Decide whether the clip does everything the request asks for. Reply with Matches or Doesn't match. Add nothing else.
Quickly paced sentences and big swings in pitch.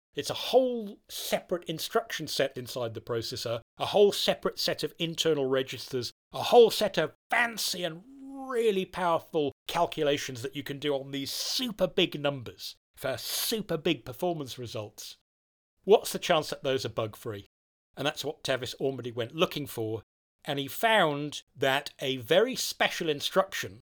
Doesn't match